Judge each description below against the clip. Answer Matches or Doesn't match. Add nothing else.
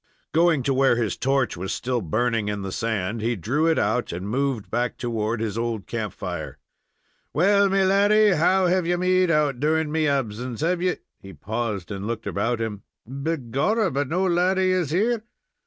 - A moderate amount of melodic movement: Doesn't match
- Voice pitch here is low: Matches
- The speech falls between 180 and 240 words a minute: Matches